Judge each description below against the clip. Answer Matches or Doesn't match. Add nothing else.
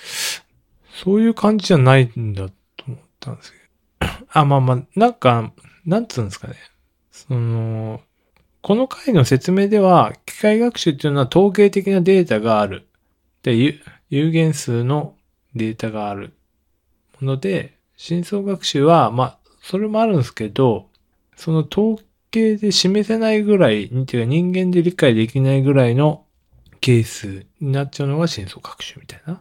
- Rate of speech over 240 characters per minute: Matches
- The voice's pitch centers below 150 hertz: Matches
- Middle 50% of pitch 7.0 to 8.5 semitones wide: Matches